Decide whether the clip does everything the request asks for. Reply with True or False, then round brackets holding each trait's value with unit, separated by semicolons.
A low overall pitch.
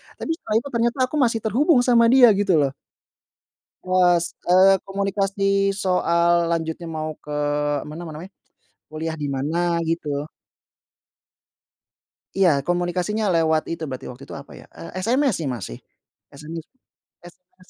False (175 Hz)